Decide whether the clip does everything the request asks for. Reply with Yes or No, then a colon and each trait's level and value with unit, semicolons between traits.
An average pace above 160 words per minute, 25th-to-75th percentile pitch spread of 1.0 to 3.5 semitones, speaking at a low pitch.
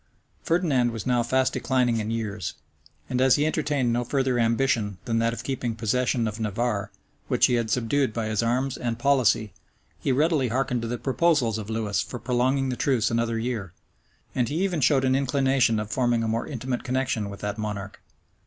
Yes: average, 190 wpm; average, 2.8 semitones; low, 120 Hz